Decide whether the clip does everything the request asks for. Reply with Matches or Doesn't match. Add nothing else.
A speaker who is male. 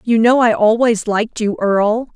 Doesn't match